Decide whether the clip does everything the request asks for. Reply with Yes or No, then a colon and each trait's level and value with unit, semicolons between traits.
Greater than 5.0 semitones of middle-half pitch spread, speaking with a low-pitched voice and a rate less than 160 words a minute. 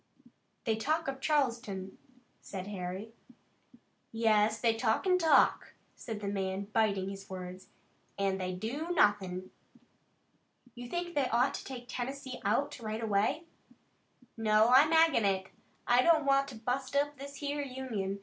No: wide, 5.6 semitones; high, 230 Hz; average, 145 wpm